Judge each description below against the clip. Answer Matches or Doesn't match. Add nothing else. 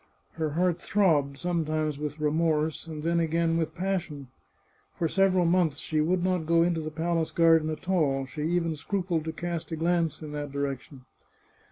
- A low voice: Doesn't match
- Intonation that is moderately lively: Doesn't match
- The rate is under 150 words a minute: Doesn't match